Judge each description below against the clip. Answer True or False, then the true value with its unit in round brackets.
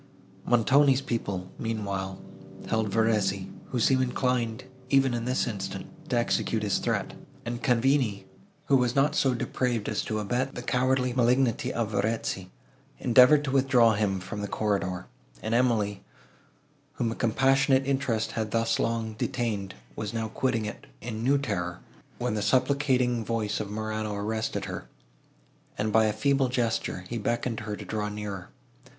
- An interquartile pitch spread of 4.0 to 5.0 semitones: False (3.2 semitones)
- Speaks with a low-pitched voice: True (115 Hz)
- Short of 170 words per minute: True (155 wpm)